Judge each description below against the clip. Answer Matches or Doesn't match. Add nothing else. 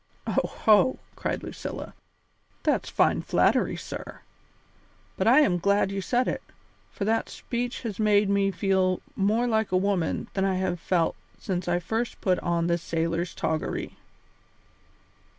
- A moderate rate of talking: Matches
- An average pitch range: Matches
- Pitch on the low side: Doesn't match